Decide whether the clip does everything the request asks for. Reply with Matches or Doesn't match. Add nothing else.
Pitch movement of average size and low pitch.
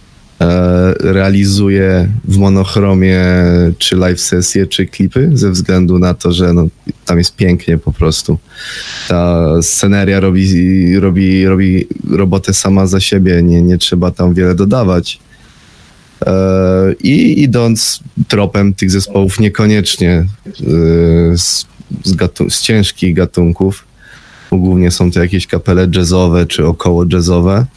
Doesn't match